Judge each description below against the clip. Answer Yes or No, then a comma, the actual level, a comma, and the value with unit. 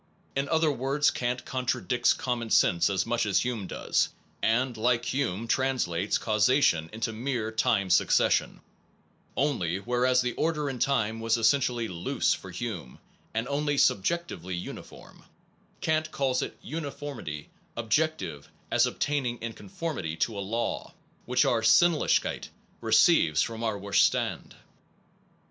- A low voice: Yes, low, 120 Hz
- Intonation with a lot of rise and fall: No, average, 4.8 semitones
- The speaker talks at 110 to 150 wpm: Yes, slow, 135 wpm